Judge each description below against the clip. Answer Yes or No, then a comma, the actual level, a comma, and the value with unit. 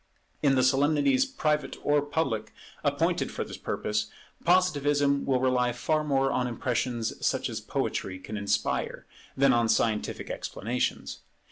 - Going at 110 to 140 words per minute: Yes, slow, 135 wpm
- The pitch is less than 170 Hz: Yes, low, 135 Hz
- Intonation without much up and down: No, average, 3.6 semitones